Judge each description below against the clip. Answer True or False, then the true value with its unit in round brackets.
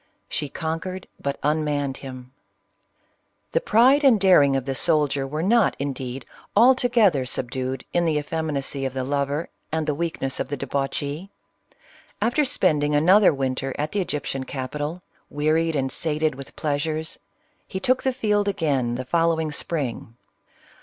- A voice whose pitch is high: False (150 Hz)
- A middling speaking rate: True (145 wpm)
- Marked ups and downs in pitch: False (4.2 semitones)